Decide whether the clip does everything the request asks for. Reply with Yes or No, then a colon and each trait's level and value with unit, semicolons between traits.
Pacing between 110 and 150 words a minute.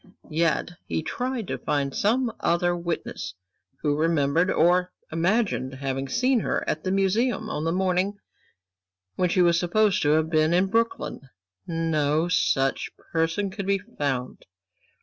Yes: average, 145 wpm